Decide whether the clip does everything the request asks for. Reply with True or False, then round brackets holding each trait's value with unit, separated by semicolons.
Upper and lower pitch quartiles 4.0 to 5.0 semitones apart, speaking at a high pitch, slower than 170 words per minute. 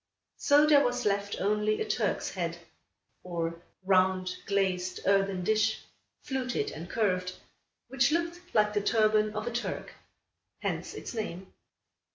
True (4.5 semitones; 210 Hz; 135 wpm)